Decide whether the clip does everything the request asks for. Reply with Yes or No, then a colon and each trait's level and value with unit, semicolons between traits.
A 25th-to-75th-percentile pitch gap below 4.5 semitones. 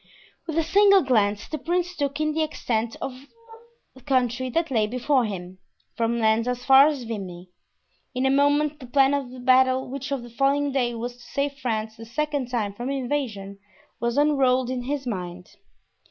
Yes: average, 3.7 semitones